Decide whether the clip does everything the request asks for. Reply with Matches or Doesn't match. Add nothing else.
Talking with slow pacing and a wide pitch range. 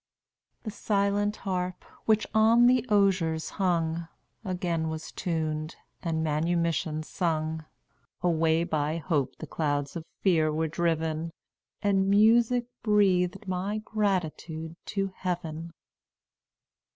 Doesn't match